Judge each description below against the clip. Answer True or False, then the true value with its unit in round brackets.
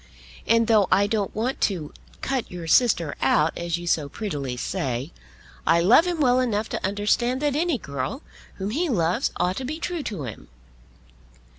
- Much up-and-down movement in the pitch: True (7.2 semitones)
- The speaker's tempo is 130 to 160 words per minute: False (175 wpm)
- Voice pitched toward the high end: True (205 Hz)